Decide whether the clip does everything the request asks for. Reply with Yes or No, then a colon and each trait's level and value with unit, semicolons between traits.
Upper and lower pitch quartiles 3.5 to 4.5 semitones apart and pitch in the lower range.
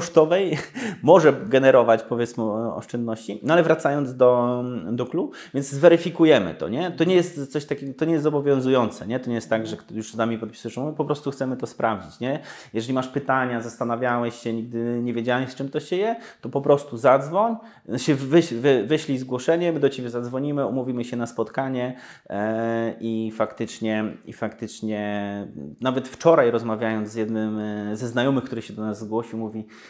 Yes: average, 3.8 semitones; low, 125 Hz